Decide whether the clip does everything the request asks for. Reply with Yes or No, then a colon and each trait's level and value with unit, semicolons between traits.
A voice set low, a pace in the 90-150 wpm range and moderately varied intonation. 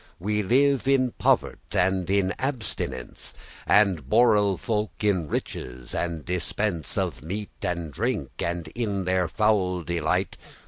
Yes: very low, 95 Hz; slow, 135 wpm; average, 3.7 semitones